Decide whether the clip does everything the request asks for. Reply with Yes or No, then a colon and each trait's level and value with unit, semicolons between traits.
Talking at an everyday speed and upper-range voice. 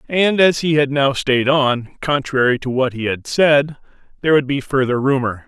No: average, 195 wpm; low, 135 Hz